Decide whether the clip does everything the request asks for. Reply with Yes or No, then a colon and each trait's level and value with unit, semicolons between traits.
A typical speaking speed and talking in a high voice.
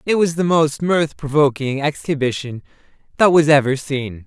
No: average, 155 wpm; medium, 145 Hz